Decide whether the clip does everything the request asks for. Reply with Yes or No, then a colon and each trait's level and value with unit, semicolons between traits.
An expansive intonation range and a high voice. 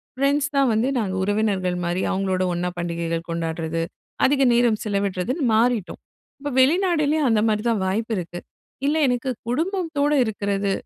Yes: wide, 6.8 semitones; high, 220 Hz